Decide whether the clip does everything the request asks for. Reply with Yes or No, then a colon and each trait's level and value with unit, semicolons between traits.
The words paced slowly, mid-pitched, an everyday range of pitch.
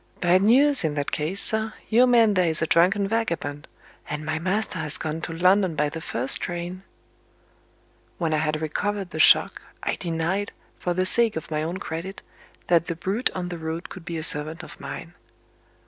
No: average, 195 wpm; medium, 175 Hz; average, 3.6 semitones